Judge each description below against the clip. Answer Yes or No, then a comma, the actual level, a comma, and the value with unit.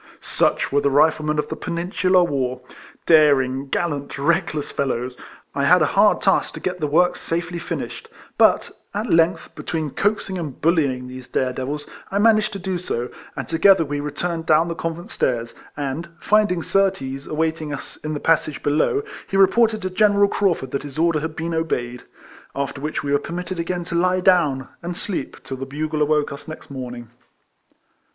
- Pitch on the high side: No, medium, 160 Hz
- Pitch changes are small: No, average, 4.1 semitones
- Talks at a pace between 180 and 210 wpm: Yes, average, 185 wpm